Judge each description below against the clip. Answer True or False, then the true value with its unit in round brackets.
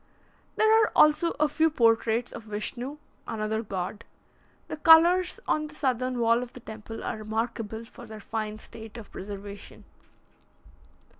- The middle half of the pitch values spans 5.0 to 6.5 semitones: True (5.5 semitones)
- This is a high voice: True (230 Hz)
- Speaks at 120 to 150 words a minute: True (145 wpm)